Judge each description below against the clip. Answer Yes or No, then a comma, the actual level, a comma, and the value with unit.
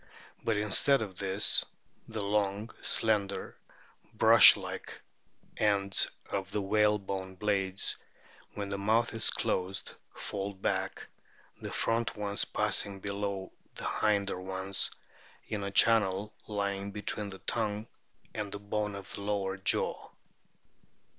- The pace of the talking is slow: Yes, slow, 120 wpm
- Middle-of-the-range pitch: No, low, 100 Hz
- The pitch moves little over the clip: Yes, narrow, 1.4 semitones